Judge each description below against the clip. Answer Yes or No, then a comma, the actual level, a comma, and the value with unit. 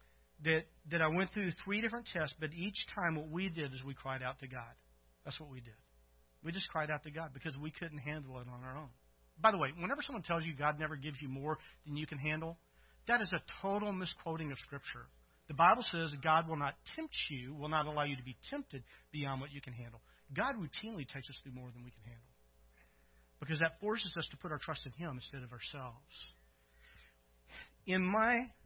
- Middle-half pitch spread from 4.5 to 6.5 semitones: Yes, average, 5.0 semitones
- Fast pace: Yes, fast, 220 wpm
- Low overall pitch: No, medium, 150 Hz